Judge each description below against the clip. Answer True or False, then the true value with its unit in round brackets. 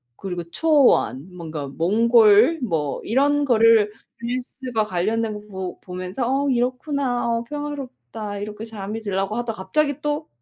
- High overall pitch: True (225 Hz)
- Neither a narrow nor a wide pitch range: True (4.9 semitones)